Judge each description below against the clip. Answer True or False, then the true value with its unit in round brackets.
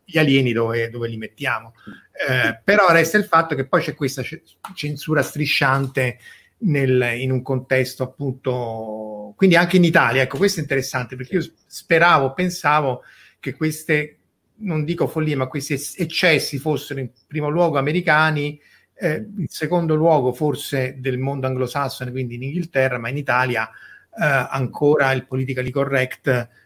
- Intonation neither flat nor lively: True (3.4 semitones)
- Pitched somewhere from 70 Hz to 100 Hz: False (140 Hz)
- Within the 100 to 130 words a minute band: False (150 wpm)